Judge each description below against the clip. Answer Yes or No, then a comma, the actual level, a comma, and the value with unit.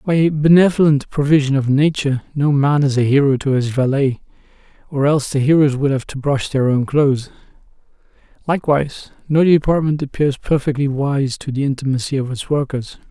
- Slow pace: No, average, 170 wpm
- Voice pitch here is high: No, medium, 140 Hz